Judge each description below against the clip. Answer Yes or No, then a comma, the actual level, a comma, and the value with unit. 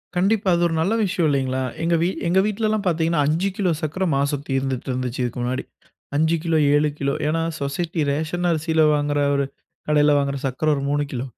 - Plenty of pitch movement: No, average, 3.7 semitones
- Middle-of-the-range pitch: Yes, medium, 155 Hz